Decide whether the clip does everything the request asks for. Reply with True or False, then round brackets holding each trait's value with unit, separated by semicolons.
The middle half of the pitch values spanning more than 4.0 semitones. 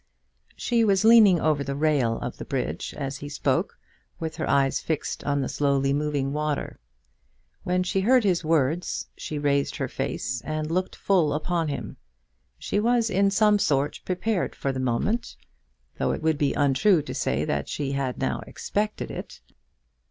True (5.2 semitones)